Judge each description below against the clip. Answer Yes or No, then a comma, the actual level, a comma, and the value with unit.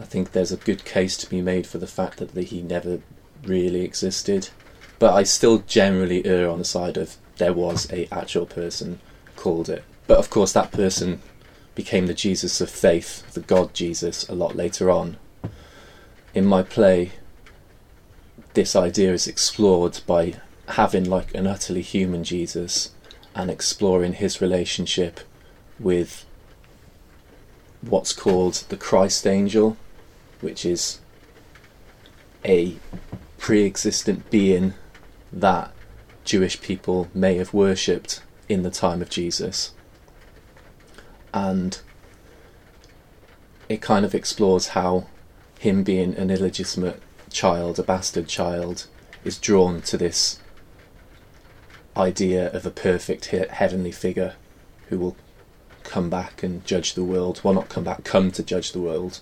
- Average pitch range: No, narrow, 1.5 semitones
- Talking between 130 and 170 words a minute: Yes, slow, 135 wpm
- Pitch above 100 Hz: No, very low, 90 Hz